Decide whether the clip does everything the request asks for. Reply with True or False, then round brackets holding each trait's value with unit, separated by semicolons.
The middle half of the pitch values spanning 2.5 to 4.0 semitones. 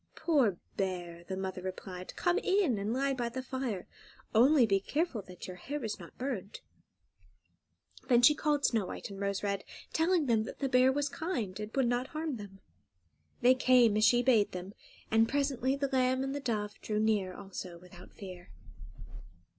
False (5.5 semitones)